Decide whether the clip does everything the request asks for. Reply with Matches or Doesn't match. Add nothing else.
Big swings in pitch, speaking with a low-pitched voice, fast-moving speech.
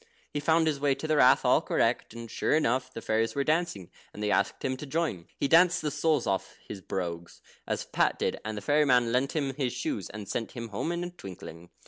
Matches